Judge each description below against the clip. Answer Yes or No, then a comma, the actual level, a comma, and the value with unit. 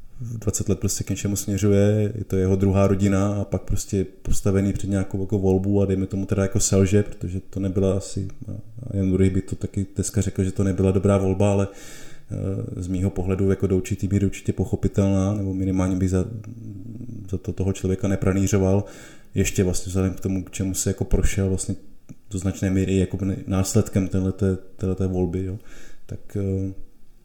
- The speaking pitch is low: Yes, very low, 95 Hz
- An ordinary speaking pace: No, fast, 180 wpm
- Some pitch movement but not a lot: No, narrow, 1.1 semitones